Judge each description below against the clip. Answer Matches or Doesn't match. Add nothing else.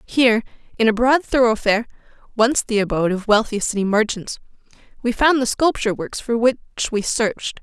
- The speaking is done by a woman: Matches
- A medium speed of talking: Matches